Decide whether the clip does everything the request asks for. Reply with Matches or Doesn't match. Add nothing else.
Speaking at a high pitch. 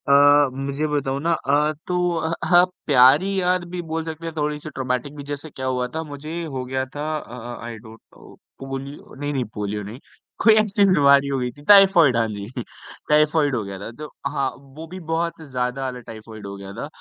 Doesn't match